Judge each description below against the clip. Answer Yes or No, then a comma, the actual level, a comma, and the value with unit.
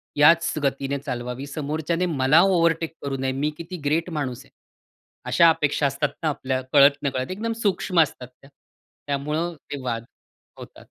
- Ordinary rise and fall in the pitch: Yes, average, 3.5 semitones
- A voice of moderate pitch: Yes, medium, 145 Hz